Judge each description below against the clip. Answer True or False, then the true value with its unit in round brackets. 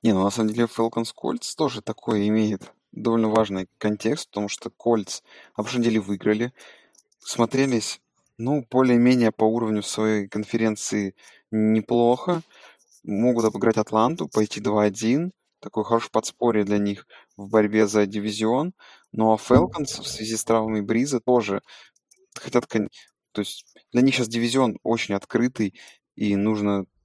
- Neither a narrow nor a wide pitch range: False (2.1 semitones)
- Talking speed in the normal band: True (140 wpm)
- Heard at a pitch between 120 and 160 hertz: False (110 Hz)